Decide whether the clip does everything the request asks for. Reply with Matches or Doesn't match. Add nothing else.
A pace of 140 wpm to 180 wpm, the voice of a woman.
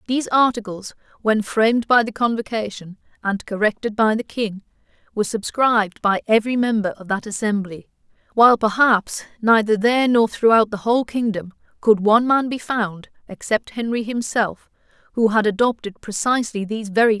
Matches